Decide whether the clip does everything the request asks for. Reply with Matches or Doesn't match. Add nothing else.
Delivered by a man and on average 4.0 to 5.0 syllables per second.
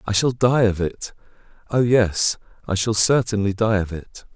Matches